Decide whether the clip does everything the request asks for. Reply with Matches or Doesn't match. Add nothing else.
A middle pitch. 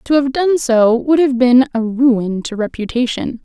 Doesn't match